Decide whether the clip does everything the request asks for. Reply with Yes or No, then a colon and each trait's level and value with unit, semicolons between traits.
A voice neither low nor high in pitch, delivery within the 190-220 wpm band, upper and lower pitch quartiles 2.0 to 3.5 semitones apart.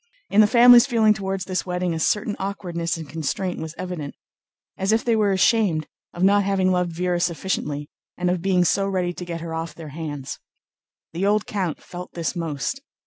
Yes: medium, 180 Hz; average, 195 wpm; average, 3.1 semitones